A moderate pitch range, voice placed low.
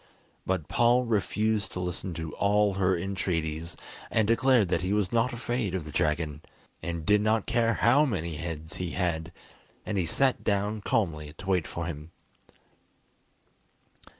Yes: average, 4.8 semitones; very low, 95 Hz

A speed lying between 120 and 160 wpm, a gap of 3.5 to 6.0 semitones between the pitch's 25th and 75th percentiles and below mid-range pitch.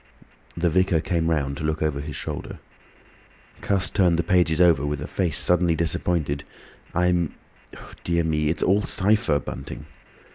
No: average, 145 wpm; average, 2.7 semitones; very low, 85 Hz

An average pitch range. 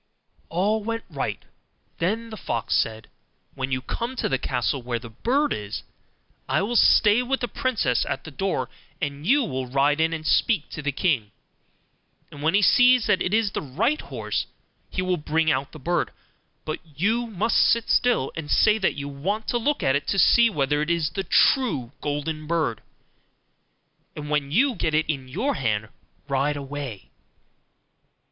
No: wide, 7.9 semitones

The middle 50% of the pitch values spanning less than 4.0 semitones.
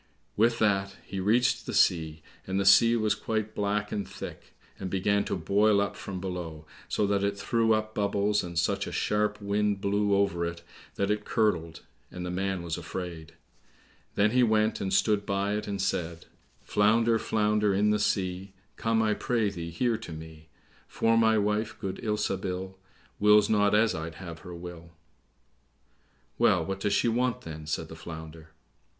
Yes: average, 3.0 semitones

